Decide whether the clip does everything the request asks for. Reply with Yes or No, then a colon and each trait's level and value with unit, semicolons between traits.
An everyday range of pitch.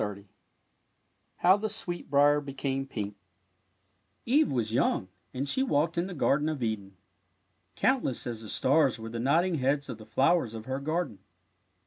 No: wide, 6.3 semitones